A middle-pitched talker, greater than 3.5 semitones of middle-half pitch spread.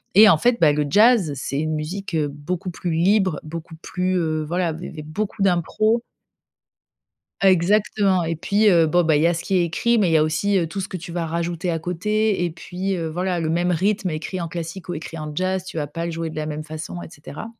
No: medium, 170 Hz; average, 3.0 semitones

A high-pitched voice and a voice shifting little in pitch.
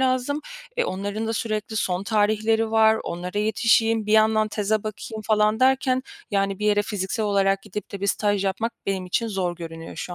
Yes: high, 210 Hz; narrow, 2.1 semitones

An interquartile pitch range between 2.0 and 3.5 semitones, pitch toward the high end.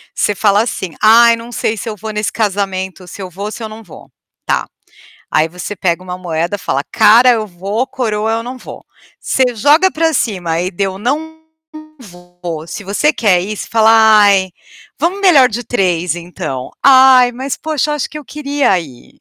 No: wide, 5.4 semitones; high, 210 Hz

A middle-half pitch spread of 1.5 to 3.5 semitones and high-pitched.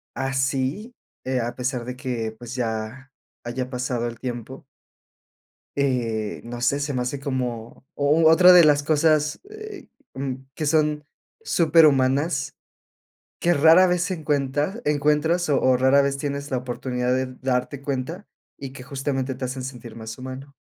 No: average, 2.9 semitones; low, 135 Hz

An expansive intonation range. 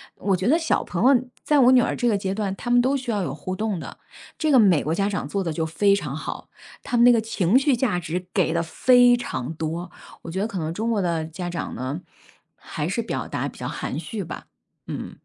Yes: wide, 6.4 semitones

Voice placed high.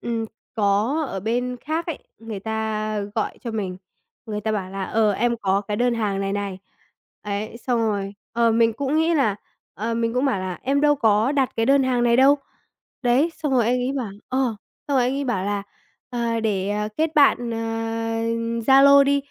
Yes: high, 230 Hz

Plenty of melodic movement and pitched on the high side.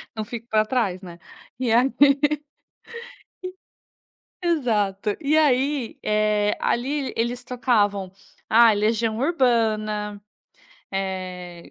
No: average, 3.5 semitones; high, 225 Hz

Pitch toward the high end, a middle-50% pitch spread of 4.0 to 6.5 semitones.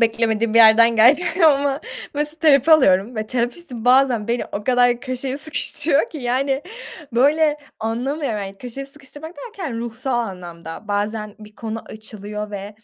Yes: high, 240 Hz; average, 4.5 semitones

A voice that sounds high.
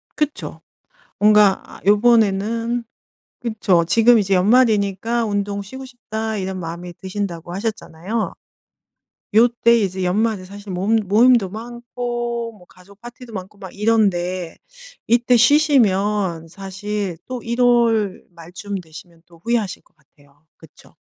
Yes: high, 205 Hz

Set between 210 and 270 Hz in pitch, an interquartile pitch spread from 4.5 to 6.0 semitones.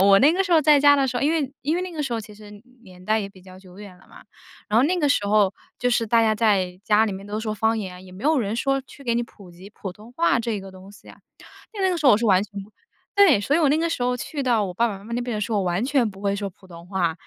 Yes: high, 220 Hz; wide, 5.6 semitones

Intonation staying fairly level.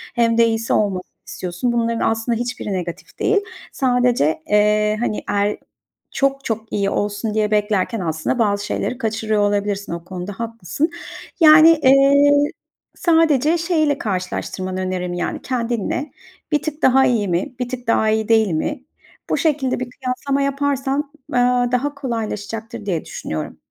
No: average, 4.7 semitones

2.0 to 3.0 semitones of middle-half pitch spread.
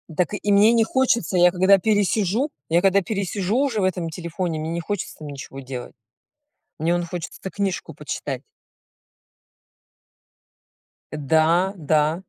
No: average, 3.9 semitones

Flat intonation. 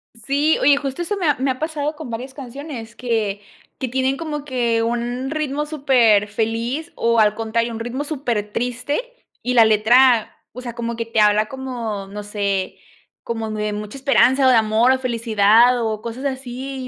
No: average, 3.2 semitones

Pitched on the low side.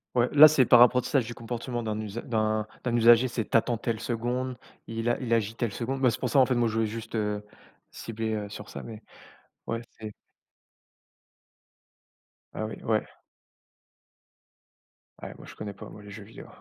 Yes: low, 115 Hz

